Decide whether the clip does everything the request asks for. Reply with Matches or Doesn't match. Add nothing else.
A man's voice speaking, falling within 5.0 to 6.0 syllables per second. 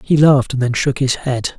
Matches